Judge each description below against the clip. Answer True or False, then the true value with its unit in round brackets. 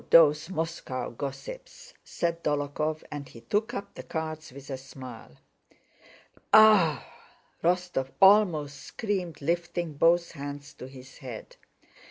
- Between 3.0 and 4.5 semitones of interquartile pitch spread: True (3.8 semitones)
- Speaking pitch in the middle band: True (155 Hz)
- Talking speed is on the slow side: True (125 wpm)